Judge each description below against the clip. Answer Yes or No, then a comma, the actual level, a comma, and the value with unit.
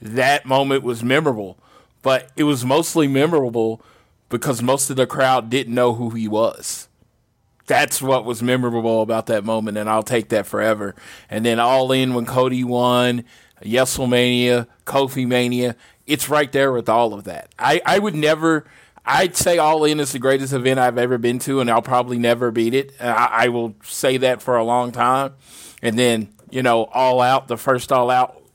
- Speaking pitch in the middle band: No, low, 125 Hz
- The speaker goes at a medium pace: Yes, average, 185 wpm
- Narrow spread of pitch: Yes, narrow, 2.1 semitones